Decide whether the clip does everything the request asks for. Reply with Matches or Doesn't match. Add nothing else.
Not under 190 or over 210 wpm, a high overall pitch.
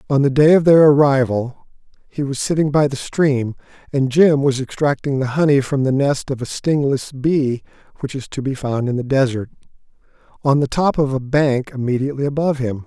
Doesn't match